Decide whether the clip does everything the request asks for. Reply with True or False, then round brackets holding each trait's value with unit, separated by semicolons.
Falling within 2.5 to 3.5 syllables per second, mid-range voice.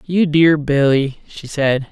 True (3.4 syllables/s; 150 Hz)